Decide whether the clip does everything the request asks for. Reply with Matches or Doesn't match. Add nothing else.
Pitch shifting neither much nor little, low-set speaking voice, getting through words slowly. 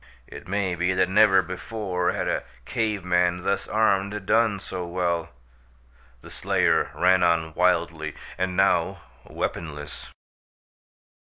Doesn't match